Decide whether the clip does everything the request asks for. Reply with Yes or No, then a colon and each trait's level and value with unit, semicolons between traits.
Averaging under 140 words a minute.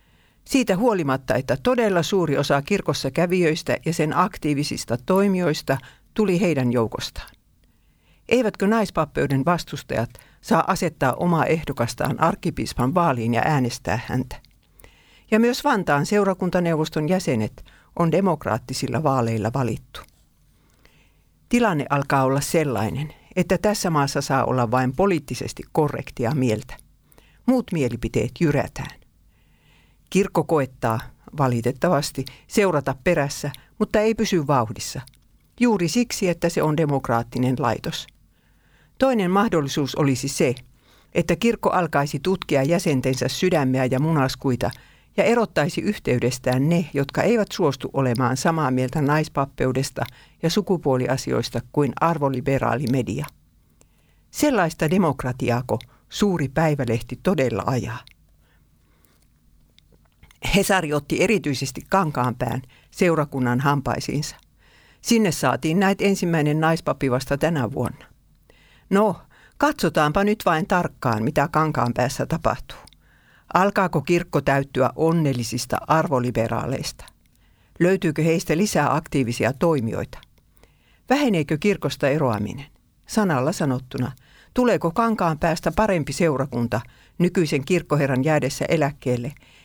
Yes: average, 100 wpm